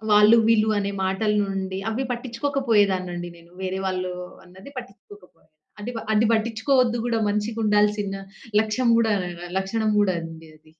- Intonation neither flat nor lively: Yes, average, 3.2 semitones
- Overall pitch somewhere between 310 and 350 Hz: No, high, 210 Hz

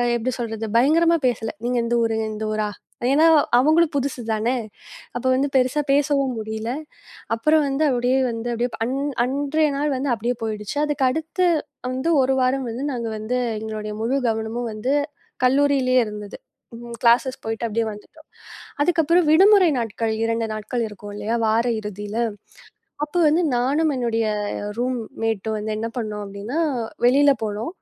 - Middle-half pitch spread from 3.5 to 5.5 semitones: Yes, average, 4.2 semitones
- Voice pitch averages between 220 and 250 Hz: Yes, high, 245 Hz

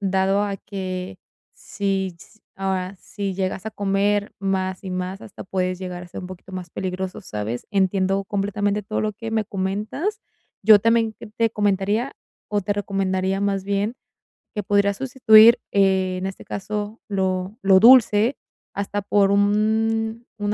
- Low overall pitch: No, high, 200 Hz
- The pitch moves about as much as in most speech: No, narrow, 1.8 semitones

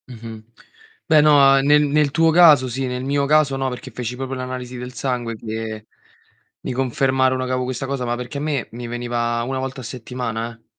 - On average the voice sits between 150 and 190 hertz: No, low, 130 Hz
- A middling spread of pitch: No, narrow, 2.1 semitones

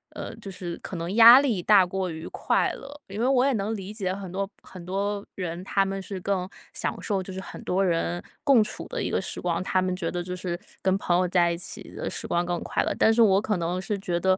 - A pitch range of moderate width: No, narrow, 2.3 semitones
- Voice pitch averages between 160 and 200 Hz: Yes, high, 190 Hz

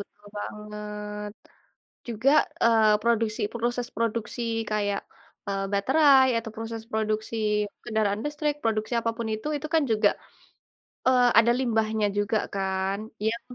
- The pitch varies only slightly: Yes, narrow, 2.0 semitones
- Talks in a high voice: Yes, high, 220 Hz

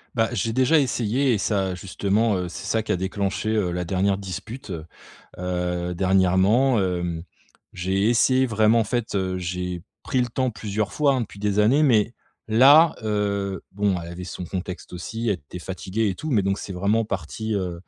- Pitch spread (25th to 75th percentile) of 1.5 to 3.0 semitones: No, average, 3.5 semitones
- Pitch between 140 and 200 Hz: No, low, 100 Hz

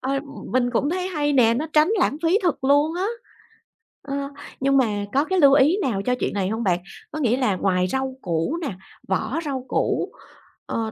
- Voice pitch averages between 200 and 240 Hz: No, very high, 265 Hz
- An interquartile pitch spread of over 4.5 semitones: Yes, average, 5.2 semitones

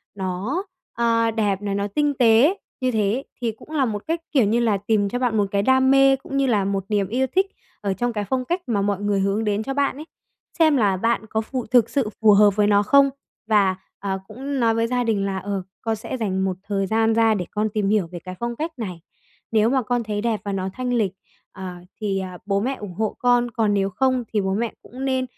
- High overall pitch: Yes, high, 220 Hz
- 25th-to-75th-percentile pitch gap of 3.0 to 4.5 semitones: Yes, average, 3.8 semitones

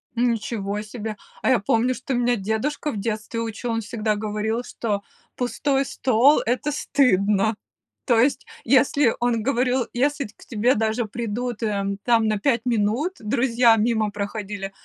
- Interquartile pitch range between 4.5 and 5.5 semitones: No, average, 2.9 semitones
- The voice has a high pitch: Yes, high, 230 Hz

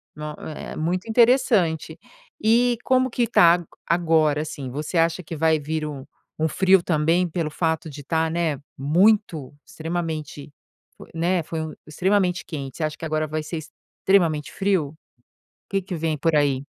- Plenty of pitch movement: No, average, 3.0 semitones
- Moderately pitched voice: Yes, medium, 160 Hz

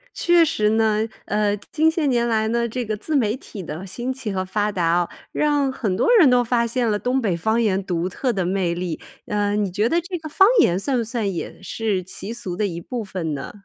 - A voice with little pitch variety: No, average, 4.7 semitones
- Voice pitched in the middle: No, high, 215 Hz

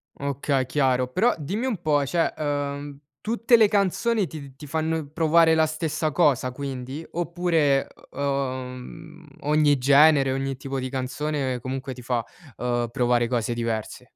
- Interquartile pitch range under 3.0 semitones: No, average, 3.6 semitones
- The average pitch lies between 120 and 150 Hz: Yes, medium, 140 Hz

